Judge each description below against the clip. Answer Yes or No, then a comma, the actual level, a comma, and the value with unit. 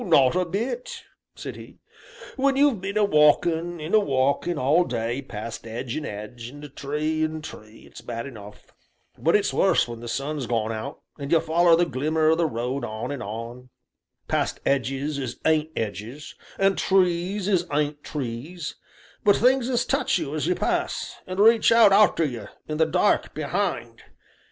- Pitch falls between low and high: Yes, medium, 150 Hz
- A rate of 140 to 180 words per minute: Yes, average, 175 wpm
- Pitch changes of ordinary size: No, wide, 6.6 semitones